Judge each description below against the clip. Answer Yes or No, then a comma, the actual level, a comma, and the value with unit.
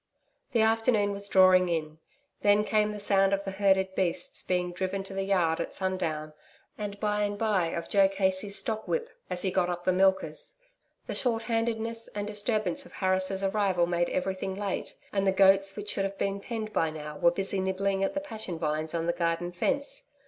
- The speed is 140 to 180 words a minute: No, average, 190 wpm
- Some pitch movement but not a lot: No, narrow, 2.3 semitones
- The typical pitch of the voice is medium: No, high, 195 Hz